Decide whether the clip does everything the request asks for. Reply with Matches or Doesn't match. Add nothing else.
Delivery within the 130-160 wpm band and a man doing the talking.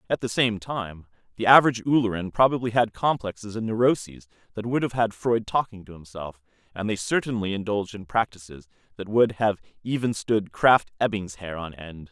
Doesn't match